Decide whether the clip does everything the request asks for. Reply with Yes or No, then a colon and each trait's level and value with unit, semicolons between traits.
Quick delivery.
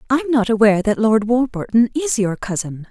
No: average, 185 wpm